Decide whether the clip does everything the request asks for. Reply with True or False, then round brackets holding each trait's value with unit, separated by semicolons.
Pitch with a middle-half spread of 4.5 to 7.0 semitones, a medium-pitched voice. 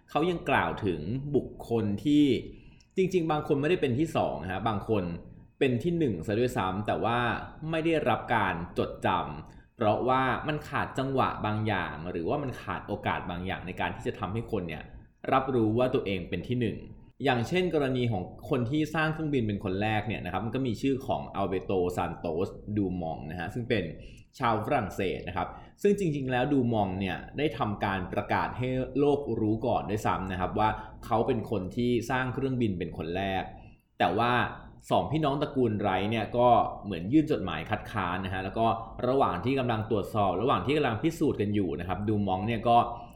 False (5.0 semitones; 115 Hz)